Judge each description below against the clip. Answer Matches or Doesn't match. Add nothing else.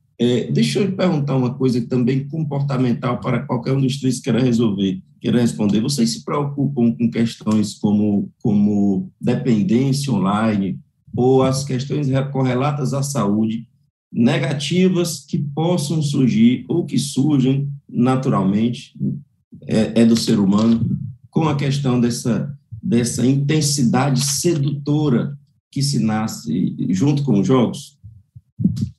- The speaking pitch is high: Doesn't match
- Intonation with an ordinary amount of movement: Matches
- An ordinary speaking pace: Doesn't match